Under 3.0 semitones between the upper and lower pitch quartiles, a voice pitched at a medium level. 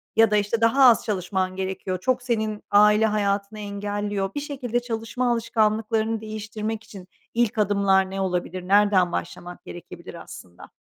No: narrow, 2.6 semitones; high, 210 Hz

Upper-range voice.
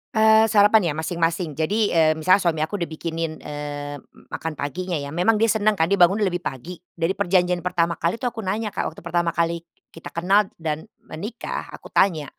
No: medium, 175 Hz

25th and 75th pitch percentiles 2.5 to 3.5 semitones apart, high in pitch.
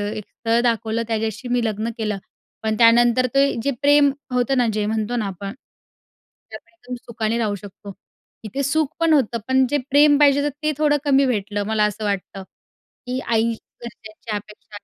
No: average, 3.9 semitones; high, 230 Hz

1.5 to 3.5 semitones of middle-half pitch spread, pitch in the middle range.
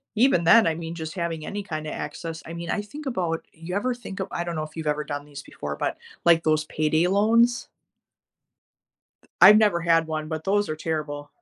No: average, 4.4 semitones; medium, 165 Hz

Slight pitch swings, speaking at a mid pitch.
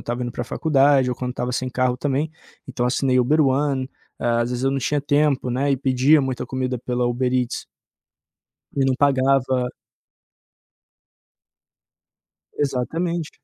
No: narrow, 2.1 semitones; low, 130 Hz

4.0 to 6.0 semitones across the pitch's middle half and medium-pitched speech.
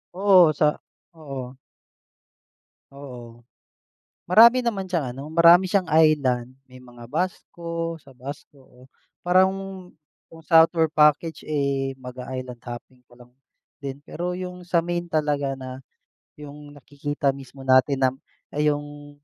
Yes: average, 4.4 semitones; medium, 145 Hz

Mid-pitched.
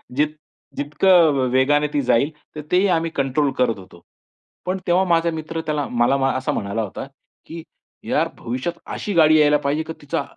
Yes: medium, 150 Hz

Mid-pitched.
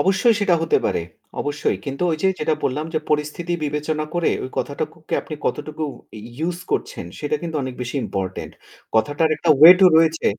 Yes: medium, 155 Hz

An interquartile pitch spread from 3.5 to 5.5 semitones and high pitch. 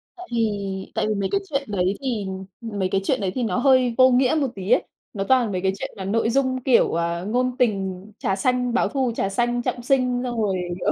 Yes: average, 4.5 semitones; high, 235 Hz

